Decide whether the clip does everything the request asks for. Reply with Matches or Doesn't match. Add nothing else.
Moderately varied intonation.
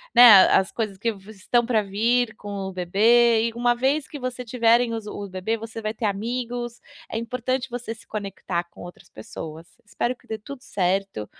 Matches